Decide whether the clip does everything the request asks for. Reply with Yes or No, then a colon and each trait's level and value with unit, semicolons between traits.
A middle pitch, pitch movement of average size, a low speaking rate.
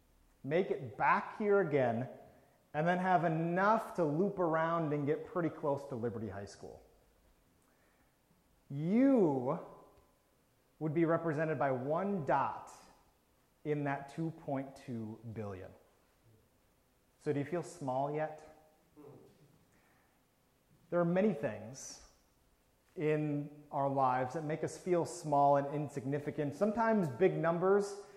Yes: medium, 150 Hz; average, 4.1 semitones; slow, 115 wpm